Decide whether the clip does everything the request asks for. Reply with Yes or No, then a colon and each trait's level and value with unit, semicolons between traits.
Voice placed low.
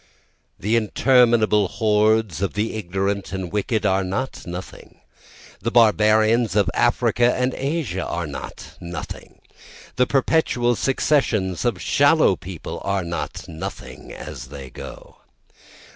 Yes: low, 105 Hz